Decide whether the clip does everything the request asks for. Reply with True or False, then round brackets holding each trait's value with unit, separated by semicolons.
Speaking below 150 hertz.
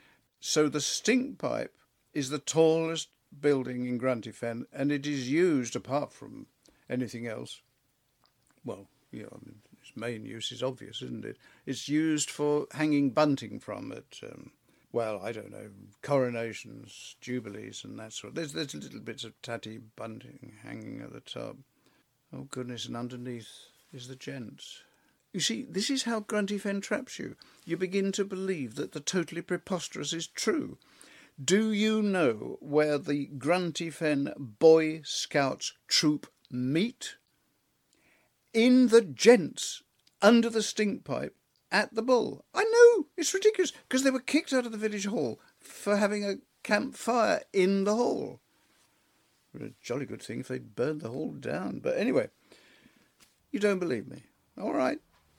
False (160 Hz)